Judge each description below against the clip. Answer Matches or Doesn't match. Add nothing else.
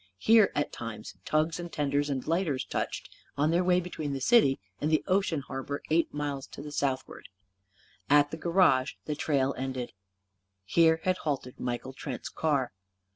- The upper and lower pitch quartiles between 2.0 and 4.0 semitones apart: Matches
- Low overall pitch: Doesn't match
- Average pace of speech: Matches